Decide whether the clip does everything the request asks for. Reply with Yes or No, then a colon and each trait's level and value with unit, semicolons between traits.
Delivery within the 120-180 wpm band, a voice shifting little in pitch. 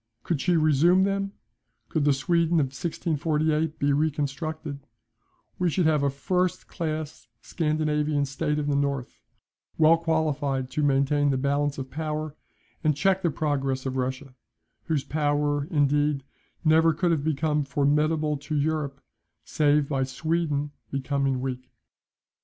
Yes: slow, 135 wpm; narrow, 2.1 semitones